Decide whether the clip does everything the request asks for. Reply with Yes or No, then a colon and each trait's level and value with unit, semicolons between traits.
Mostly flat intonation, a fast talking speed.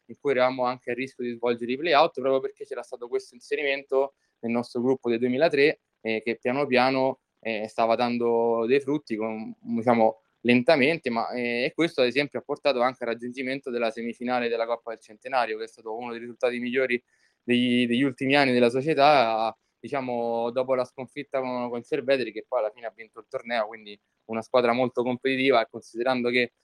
Yes: narrow, 2.3 semitones; fast, 195 wpm